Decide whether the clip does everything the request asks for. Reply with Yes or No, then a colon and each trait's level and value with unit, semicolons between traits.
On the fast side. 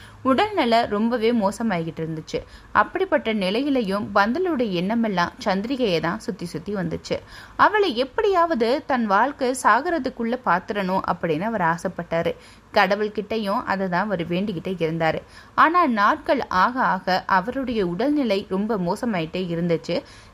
No: average, 105 wpm